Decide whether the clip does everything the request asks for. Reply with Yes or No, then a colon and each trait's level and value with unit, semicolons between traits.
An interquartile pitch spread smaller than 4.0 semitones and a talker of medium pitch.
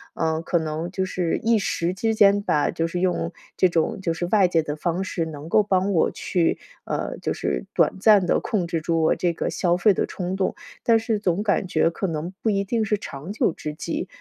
Yes: average, 3.4 semitones; medium, 180 Hz